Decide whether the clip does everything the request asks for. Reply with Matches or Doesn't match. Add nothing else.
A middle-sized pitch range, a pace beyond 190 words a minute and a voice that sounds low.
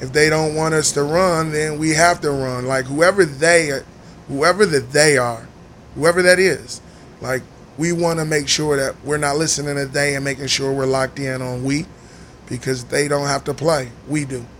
Doesn't match